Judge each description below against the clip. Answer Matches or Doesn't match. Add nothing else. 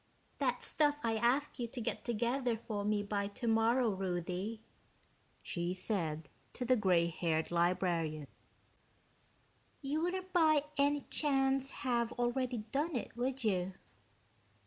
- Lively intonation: Matches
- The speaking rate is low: Matches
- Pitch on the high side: Matches